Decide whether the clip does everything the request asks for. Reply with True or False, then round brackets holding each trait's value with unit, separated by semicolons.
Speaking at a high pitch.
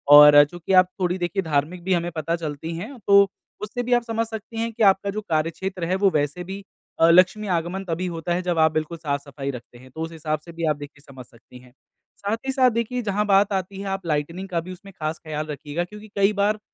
False (175 Hz)